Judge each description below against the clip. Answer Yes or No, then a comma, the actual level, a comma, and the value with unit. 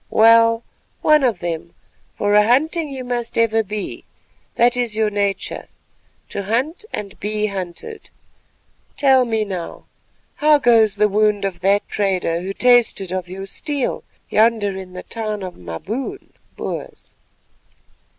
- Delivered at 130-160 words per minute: Yes, average, 140 wpm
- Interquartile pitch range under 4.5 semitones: Yes, average, 3.8 semitones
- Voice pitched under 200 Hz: No, high, 215 Hz